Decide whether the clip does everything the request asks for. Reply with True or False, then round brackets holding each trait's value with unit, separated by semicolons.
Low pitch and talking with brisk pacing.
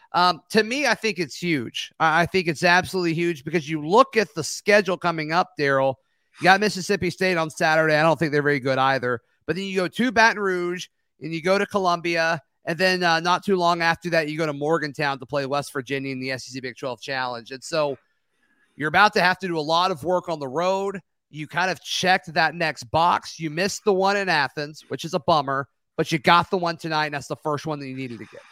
False (165 Hz; 245 wpm)